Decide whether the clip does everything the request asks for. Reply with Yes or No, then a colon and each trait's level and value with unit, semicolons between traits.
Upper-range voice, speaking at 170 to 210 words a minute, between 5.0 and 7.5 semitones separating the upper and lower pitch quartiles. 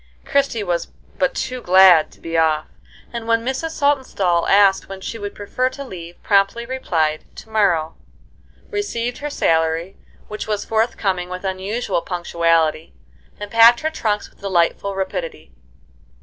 No: high, 200 Hz; average, 145 wpm; wide, 5.4 semitones